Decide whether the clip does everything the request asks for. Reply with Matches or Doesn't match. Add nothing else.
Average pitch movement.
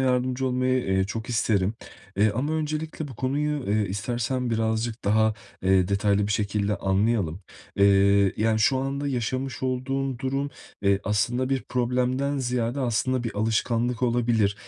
Matches